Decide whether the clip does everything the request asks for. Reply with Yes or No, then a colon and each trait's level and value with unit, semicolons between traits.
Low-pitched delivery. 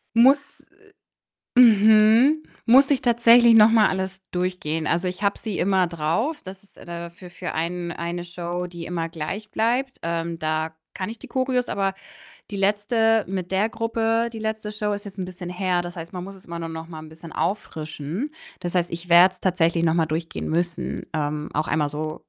No: medium, 185 Hz